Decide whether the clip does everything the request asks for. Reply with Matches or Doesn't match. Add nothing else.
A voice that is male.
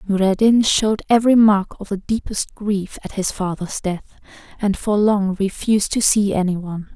Doesn't match